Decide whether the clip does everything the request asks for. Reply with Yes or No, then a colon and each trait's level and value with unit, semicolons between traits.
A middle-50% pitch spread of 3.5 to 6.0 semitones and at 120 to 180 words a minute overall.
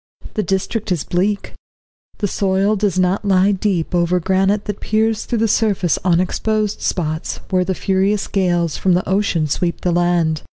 No: average, 2.7 semitones; average, 170 wpm